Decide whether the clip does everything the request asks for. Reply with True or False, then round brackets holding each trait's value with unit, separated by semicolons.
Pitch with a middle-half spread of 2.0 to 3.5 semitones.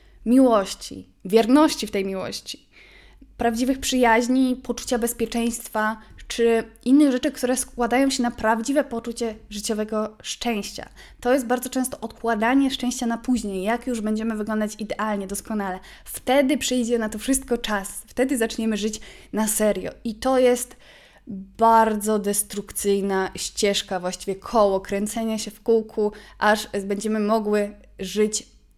True (2.8 semitones)